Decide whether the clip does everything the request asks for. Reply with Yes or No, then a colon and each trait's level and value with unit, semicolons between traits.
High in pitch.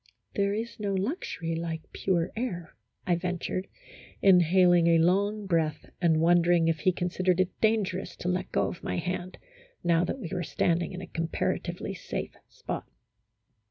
No: medium, 180 Hz